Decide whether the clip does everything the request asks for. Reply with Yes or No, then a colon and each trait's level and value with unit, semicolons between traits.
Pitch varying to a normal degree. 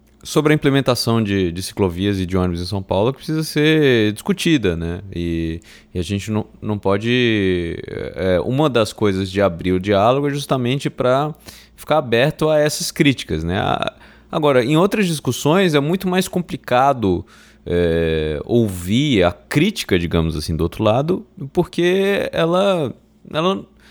No: wide, 8.7 semitones